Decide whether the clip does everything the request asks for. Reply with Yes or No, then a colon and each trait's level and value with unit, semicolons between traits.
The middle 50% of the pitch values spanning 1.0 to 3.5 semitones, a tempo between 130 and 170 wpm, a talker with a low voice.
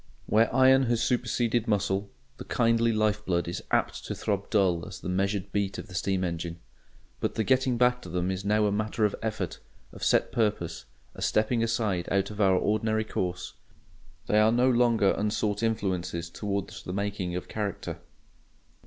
No: average, 3.2 semitones; average, 180 wpm; low, 105 Hz